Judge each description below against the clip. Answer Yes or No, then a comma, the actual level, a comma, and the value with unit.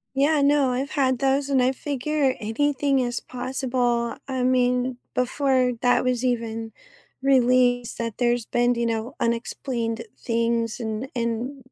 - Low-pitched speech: No, very high, 250 Hz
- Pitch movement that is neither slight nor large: No, narrow, 2.1 semitones